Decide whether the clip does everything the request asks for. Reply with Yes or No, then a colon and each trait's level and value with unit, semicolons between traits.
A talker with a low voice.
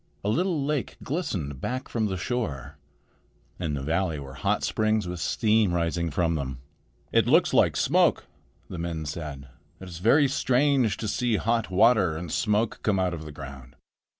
Yes: very low, 95 Hz